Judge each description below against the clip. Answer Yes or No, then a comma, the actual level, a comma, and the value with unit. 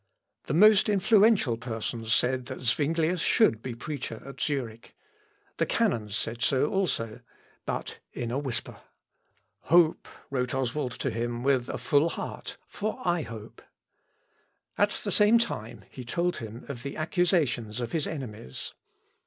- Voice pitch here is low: Yes, low, 130 Hz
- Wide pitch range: Yes, wide, 6.2 semitones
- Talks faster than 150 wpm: No, average, 145 wpm